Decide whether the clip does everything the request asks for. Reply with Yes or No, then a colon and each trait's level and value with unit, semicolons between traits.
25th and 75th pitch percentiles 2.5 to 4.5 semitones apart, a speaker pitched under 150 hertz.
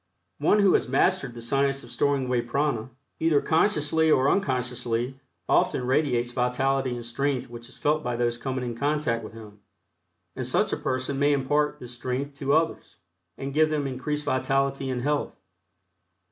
Yes: average, 3.0 semitones; low, 135 Hz